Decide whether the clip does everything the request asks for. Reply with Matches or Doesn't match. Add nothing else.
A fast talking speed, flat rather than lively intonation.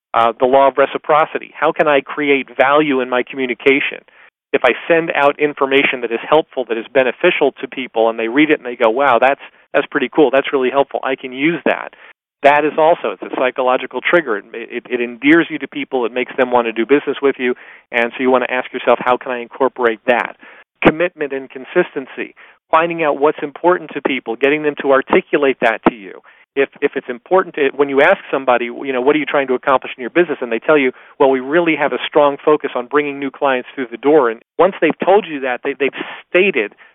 Doesn't match